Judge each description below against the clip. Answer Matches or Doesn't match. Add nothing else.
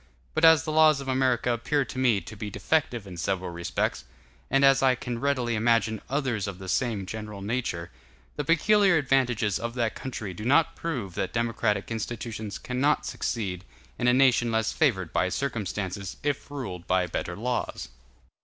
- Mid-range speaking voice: Doesn't match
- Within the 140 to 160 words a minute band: Doesn't match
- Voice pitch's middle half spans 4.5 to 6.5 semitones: Matches